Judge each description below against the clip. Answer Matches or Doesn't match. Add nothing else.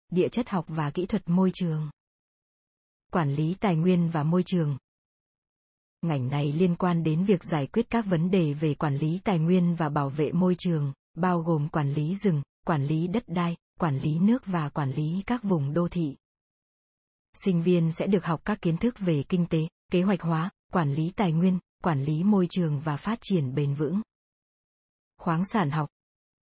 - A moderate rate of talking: Matches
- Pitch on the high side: Doesn't match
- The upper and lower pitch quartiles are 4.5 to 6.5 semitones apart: Doesn't match